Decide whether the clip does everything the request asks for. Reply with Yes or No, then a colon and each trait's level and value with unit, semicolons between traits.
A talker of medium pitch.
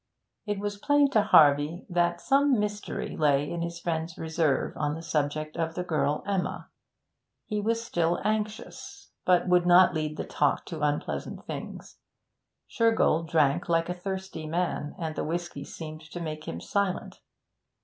Yes: medium, 170 Hz